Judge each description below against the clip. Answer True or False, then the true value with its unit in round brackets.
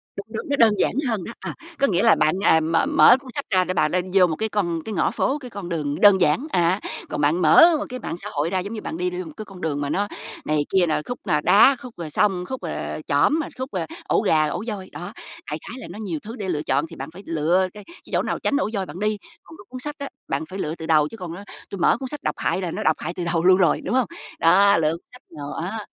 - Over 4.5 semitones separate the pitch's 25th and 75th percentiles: True (5.2 semitones)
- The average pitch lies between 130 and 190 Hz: True (185 Hz)